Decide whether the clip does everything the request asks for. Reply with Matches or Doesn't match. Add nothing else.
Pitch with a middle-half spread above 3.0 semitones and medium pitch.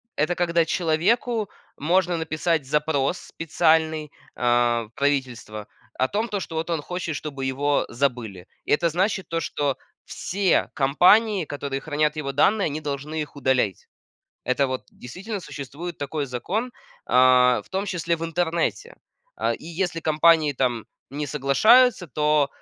Matches